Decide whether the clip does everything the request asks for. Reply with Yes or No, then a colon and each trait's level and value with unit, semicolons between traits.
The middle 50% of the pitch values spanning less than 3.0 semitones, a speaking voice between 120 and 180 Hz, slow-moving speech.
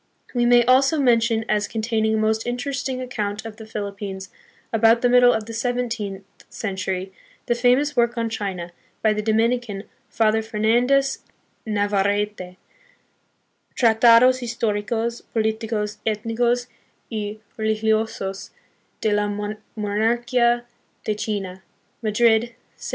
No: narrow, 2.4 semitones; high, 220 Hz; slow, 125 wpm